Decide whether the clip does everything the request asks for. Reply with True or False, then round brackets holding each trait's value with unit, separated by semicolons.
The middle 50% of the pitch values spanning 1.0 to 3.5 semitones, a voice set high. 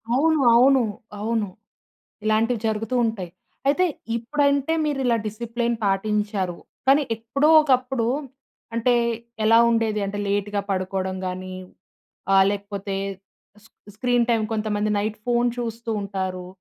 True (3.2 semitones; 225 Hz)